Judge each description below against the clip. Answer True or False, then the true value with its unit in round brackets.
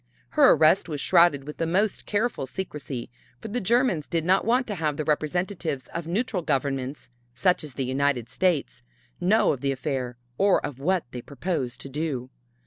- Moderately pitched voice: True (155 Hz)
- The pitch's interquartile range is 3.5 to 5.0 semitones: False (5.4 semitones)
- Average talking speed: True (180 wpm)